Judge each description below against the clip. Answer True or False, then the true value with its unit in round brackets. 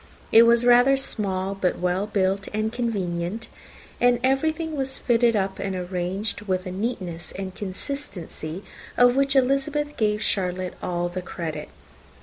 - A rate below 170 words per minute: True (140 wpm)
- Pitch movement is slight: False (5.0 semitones)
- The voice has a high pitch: True (205 Hz)